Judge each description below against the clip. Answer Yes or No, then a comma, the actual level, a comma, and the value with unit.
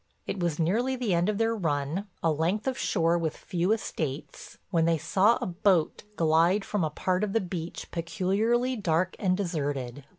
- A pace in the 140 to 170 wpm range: No, average, 185 wpm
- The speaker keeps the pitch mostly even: No, average, 4.3 semitones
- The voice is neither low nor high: Yes, medium, 180 Hz